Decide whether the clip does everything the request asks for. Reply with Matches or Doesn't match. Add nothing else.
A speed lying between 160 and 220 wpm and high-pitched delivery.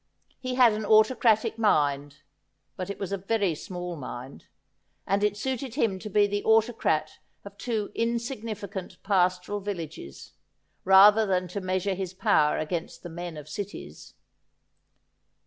Doesn't match